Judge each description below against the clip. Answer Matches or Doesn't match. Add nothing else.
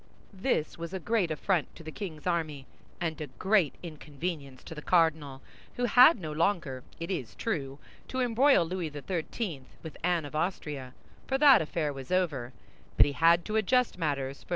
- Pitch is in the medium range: Matches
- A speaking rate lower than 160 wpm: Doesn't match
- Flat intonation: Doesn't match